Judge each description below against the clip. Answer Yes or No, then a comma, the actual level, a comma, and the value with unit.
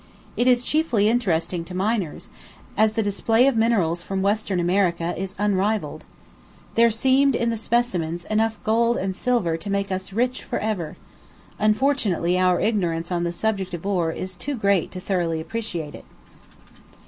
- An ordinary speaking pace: Yes, average, 160 wpm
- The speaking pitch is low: No, high, 200 Hz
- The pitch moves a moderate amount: Yes, average, 4.3 semitones